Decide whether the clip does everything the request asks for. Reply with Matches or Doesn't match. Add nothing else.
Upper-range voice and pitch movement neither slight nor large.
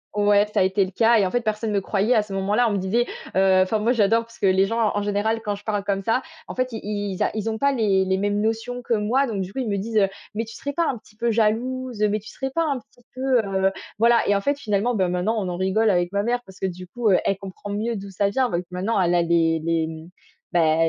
Matches